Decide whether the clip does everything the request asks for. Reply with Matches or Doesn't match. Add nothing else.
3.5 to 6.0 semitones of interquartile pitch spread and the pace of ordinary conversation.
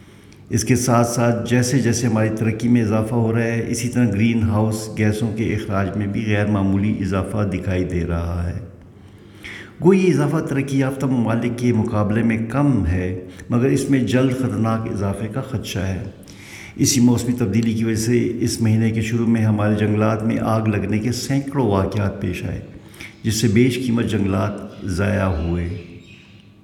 Doesn't match